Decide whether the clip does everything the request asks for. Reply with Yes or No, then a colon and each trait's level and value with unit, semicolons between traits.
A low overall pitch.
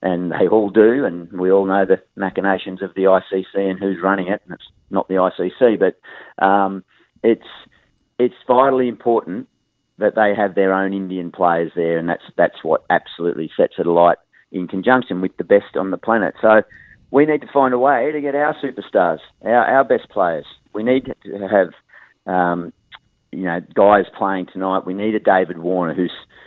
Yes: very low, 95 Hz